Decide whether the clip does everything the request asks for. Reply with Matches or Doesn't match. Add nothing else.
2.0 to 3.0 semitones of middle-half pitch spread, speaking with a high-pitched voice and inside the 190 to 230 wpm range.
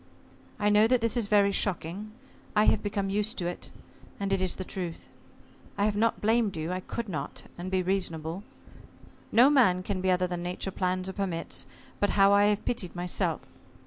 Matches